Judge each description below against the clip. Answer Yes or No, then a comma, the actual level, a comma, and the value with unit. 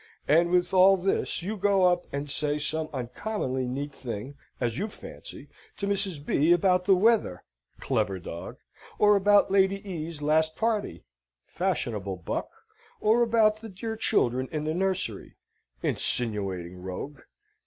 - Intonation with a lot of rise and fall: Yes, wide, 7.3 semitones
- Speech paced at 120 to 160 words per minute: Yes, average, 145 wpm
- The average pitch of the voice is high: No, medium, 165 Hz